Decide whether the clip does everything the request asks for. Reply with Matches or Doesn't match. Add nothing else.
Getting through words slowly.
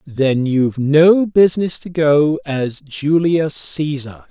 Matches